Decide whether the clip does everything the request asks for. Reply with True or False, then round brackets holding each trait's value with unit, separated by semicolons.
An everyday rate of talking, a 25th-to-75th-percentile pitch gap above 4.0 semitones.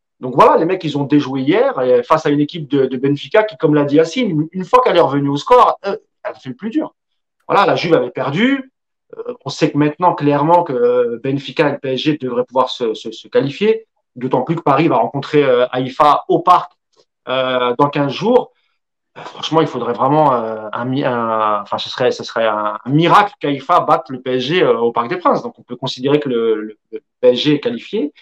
False (225 wpm; 5.2 semitones)